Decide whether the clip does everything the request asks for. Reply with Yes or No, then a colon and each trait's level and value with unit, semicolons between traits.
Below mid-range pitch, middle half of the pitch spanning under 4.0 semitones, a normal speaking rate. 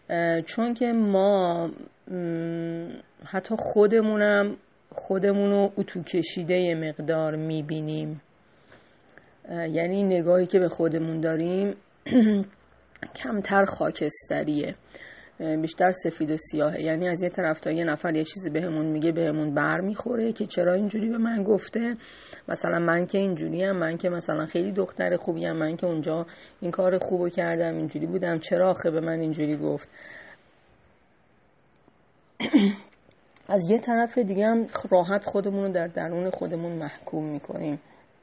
No: medium, 175 Hz; average, 3.6 semitones; average, 130 wpm